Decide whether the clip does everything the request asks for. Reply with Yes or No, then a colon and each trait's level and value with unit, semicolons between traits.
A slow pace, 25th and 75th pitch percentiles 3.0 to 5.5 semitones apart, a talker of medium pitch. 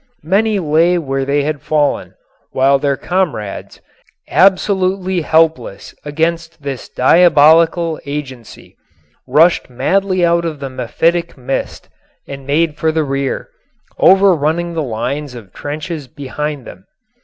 Yes: slow, 120 wpm; average, 3.7 semitones; medium, 155 Hz